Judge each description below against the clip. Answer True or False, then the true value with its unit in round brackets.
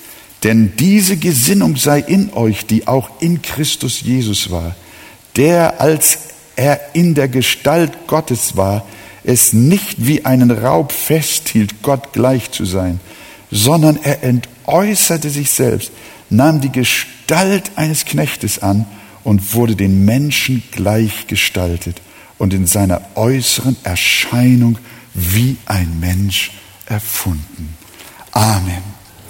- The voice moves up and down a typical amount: False (6.4 semitones)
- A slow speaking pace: True (115 wpm)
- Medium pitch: False (120 Hz)